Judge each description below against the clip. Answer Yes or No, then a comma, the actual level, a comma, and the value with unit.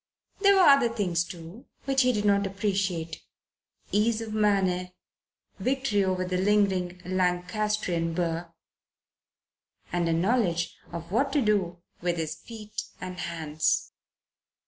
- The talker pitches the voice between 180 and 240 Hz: Yes, high, 190 Hz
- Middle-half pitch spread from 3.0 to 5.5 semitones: Yes, average, 3.5 semitones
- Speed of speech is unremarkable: No, slow, 125 wpm